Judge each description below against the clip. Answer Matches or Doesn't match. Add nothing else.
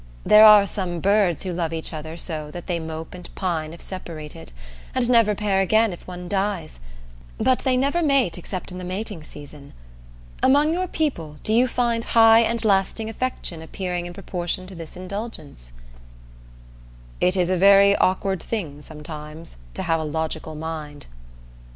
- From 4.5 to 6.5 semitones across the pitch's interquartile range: Matches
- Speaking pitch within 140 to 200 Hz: Matches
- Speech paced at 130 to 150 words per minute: Doesn't match